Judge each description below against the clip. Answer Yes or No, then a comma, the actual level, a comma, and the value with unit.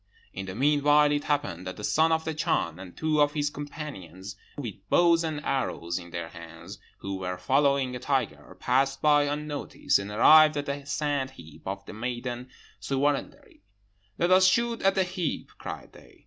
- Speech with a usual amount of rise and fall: No, wide, 7.1 semitones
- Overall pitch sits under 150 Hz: Yes, medium, 140 Hz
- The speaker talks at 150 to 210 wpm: Yes, average, 180 wpm